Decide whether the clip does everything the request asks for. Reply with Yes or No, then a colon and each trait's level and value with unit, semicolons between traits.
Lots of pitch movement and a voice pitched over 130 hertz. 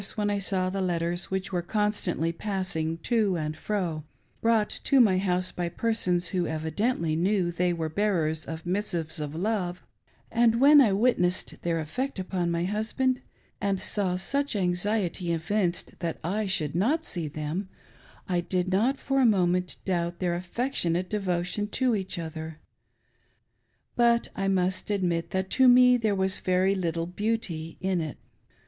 No: average, 3.5 semitones; medium, 185 Hz